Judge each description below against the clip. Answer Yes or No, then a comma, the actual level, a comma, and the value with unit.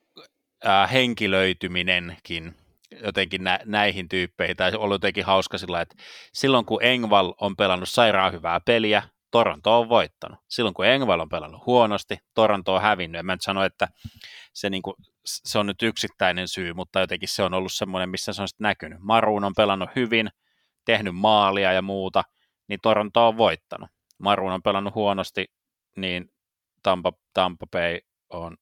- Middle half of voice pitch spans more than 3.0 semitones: No, narrow, 2.6 semitones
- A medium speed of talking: No, fast, 160 wpm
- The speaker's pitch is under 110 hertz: Yes, low, 100 Hz